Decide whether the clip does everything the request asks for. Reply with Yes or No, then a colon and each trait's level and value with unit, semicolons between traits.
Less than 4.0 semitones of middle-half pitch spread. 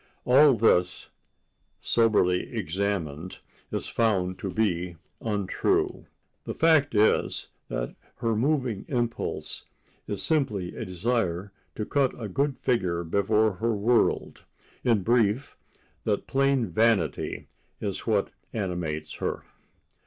No: average, 4.6 semitones